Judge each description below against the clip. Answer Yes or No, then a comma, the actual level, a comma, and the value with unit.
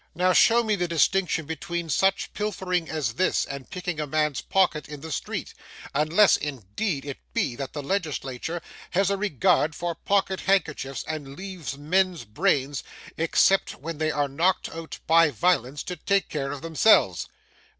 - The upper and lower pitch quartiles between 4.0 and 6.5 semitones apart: Yes, average, 4.4 semitones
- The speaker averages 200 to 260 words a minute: No, average, 160 wpm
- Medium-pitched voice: Yes, medium, 160 Hz